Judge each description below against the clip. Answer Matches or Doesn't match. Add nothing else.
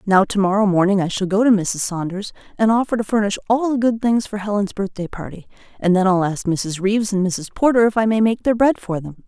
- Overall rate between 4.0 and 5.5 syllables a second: Doesn't match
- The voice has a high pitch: Matches